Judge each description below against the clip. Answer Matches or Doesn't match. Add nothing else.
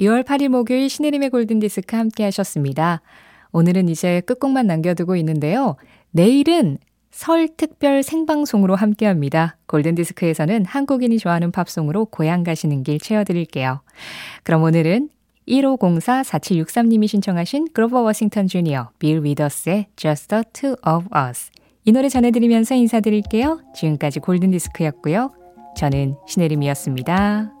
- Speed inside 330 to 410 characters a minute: Matches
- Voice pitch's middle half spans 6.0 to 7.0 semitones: Matches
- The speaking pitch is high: Matches